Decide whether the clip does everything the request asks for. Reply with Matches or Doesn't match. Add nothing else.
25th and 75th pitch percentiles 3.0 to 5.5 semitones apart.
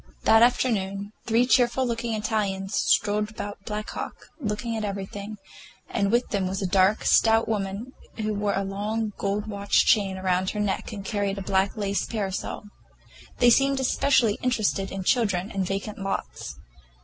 Doesn't match